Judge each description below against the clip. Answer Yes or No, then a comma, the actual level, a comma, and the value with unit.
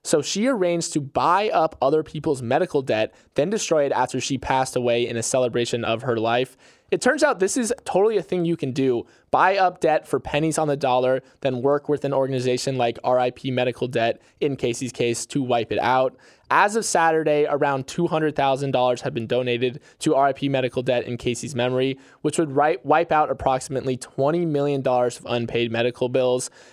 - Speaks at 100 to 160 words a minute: No, average, 190 wpm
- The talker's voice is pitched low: Yes, low, 130 Hz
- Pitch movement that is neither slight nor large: Yes, average, 3.4 semitones